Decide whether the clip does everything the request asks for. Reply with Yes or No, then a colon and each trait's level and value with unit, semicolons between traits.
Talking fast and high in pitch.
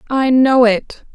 No: average, 155 wpm; very high, 250 Hz